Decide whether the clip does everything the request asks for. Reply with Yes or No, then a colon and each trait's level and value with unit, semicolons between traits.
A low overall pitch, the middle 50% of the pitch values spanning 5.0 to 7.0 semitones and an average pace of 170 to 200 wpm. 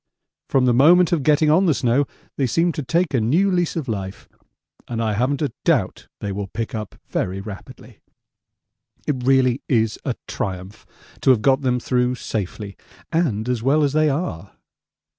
Yes: low, 125 Hz; wide, 5.6 semitones; average, 180 wpm